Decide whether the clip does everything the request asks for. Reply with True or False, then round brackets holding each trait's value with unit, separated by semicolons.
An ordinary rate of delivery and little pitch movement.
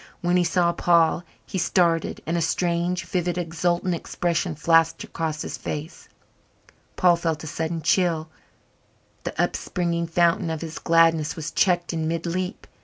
True (150 wpm; 1.4 semitones)